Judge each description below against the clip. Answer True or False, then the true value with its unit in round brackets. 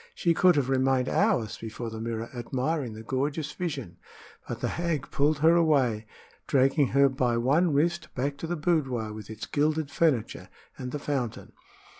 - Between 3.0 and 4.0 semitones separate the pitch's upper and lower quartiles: False (4.7 semitones)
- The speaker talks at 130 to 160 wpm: False (170 wpm)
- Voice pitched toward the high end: False (140 Hz)